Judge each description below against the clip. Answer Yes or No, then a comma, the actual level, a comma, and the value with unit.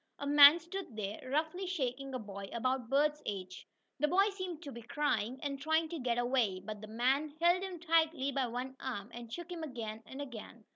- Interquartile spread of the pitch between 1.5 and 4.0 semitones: No, average, 5.2 semitones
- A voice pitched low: No, very high, 270 Hz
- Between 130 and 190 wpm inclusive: No, fast, 205 wpm